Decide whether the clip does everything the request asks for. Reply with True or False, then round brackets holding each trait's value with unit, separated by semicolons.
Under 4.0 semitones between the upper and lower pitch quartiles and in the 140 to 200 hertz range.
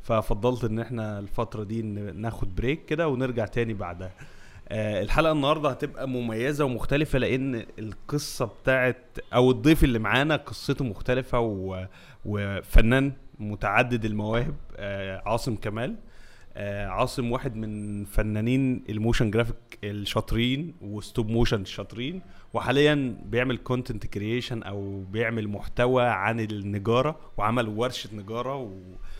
False (3.4 semitones; 115 Hz)